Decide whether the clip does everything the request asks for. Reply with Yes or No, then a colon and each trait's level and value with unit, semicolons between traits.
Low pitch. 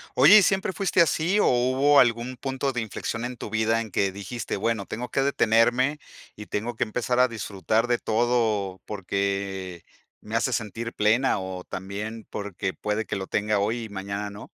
Yes: low, 110 Hz